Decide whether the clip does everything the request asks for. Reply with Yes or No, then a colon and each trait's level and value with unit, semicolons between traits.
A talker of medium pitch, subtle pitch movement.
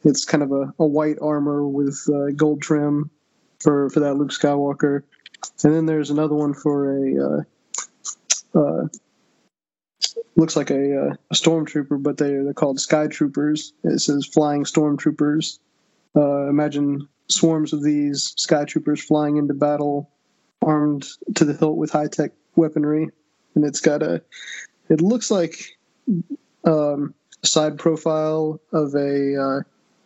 Yes: medium, 150 Hz; narrow, 1.3 semitones